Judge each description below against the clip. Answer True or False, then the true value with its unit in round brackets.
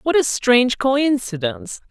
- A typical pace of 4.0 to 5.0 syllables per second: True (4.6 syllables/s)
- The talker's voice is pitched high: True (235 Hz)